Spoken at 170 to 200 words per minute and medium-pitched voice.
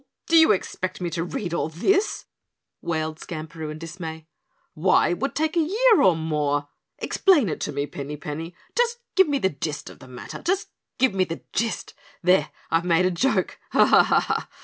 Yes: average, 190 wpm; medium, 175 Hz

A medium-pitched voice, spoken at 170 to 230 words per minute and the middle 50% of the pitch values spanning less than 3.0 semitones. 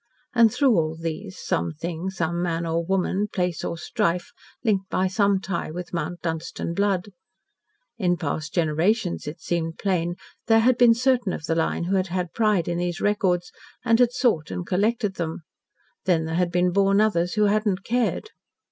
No: medium, 180 Hz; average, 180 wpm; average, 3.6 semitones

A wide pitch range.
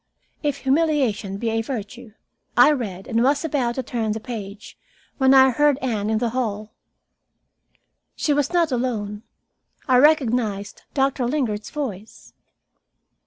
No: average, 4.3 semitones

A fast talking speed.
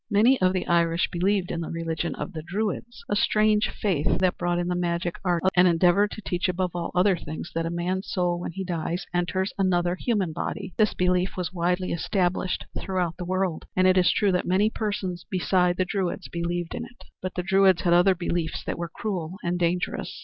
Yes: fast, 210 wpm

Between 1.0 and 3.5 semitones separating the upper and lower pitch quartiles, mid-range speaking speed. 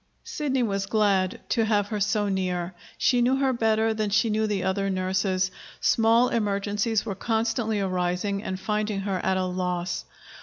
Yes: average, 2.9 semitones; average, 165 wpm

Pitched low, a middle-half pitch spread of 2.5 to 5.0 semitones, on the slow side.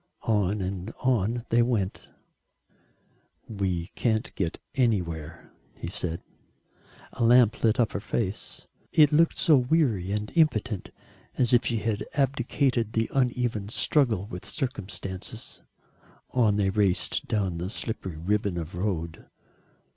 Yes: low, 105 Hz; average, 4.5 semitones; slow, 125 wpm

